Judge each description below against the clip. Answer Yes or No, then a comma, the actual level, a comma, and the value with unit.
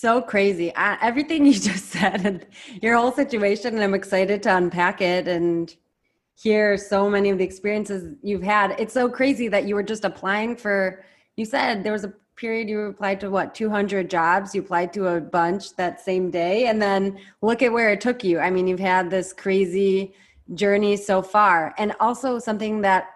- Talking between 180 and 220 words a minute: Yes, average, 195 wpm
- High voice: Yes, high, 200 Hz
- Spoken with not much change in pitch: Yes, narrow, 2.3 semitones